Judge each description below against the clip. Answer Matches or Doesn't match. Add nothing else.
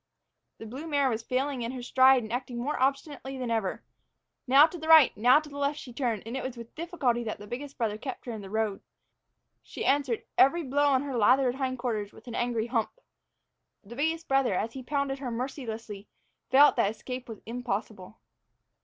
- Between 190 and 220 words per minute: Matches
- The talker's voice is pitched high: Matches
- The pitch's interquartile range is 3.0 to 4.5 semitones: Matches